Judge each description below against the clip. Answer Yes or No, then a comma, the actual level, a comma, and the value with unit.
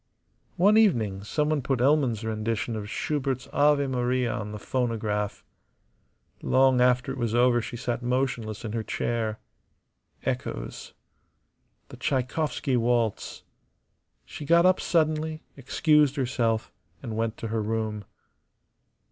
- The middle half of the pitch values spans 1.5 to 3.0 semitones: No, average, 3.9 semitones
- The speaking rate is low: Yes, slow, 120 wpm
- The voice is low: Yes, low, 125 Hz